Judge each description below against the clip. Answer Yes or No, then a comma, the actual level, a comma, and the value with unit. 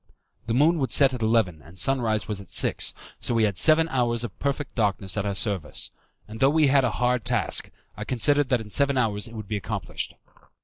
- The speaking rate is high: Yes, fast, 220 wpm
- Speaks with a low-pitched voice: Yes, low, 115 Hz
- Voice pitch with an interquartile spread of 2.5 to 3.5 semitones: No, average, 4.4 semitones